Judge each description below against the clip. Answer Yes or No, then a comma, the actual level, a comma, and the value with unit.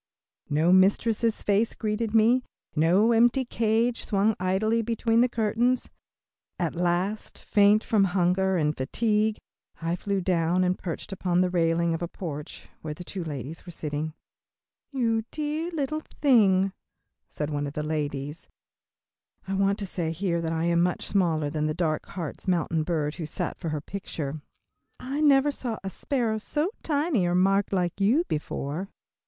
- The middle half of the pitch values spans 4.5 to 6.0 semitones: Yes, average, 5.2 semitones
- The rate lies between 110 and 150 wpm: No, average, 160 wpm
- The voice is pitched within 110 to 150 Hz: No, high, 190 Hz